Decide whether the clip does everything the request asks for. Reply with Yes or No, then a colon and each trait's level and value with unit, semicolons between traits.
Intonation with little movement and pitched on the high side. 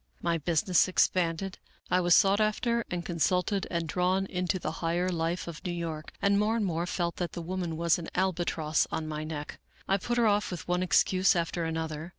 No: narrow, 2.3 semitones; medium, 175 Hz